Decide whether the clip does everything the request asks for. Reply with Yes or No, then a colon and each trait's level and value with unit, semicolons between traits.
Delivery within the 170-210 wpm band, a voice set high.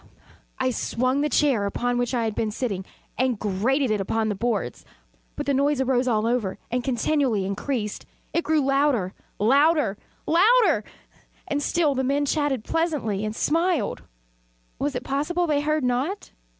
No: average, 160 wpm; very high, 260 Hz